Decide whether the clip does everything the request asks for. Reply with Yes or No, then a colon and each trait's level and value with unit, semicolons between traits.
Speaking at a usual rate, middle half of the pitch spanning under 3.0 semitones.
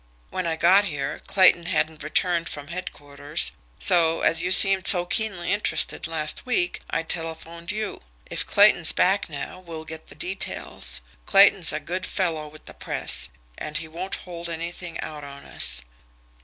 Yes: average, 160 wpm; narrow, 2.6 semitones